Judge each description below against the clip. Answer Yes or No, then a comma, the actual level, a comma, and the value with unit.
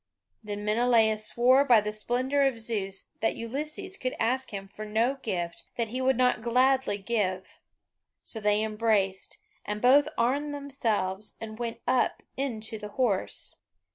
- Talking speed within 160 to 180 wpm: No, average, 150 wpm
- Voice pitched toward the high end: Yes, high, 230 Hz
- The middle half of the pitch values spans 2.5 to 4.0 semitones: Yes, average, 3.5 semitones